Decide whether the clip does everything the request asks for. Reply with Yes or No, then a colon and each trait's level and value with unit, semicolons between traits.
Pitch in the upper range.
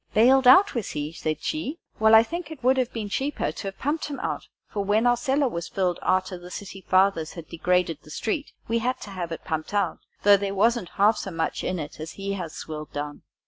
Yes: high, 200 Hz